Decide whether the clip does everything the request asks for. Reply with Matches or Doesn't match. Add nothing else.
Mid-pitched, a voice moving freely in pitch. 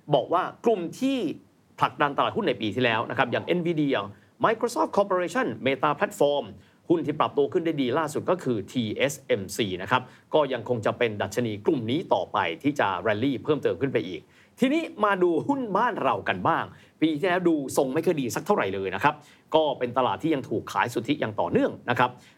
Matches